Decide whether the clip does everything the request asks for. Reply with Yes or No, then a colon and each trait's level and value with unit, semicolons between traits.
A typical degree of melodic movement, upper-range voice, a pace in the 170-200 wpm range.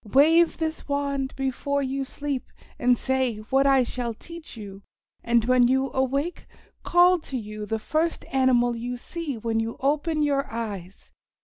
No: average, 3.3 semitones; very high, 265 Hz; average, 155 wpm